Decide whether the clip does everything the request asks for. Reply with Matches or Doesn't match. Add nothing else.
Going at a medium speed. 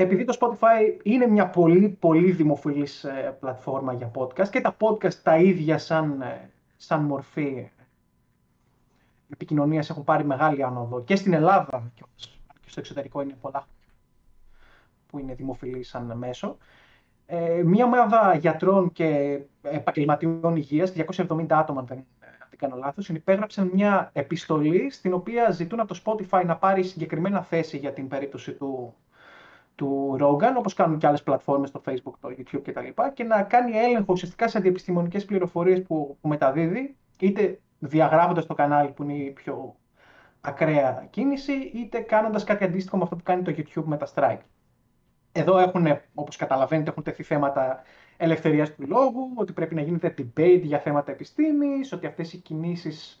Matches